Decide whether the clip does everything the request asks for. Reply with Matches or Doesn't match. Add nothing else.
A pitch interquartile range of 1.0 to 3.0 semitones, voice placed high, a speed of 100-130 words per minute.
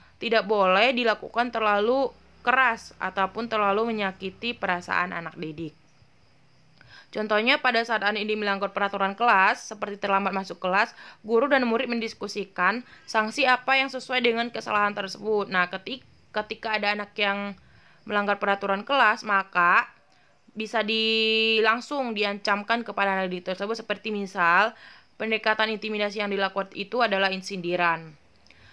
Matches